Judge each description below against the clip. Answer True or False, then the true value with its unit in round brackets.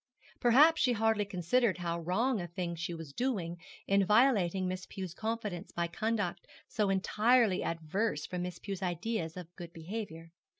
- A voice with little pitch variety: False (4.5 semitones)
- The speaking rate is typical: True (160 wpm)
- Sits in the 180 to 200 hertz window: True (190 Hz)